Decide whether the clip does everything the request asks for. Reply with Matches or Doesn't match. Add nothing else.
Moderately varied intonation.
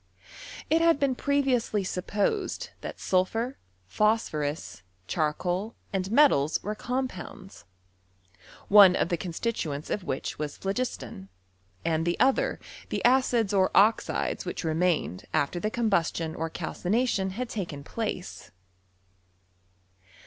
Doesn't match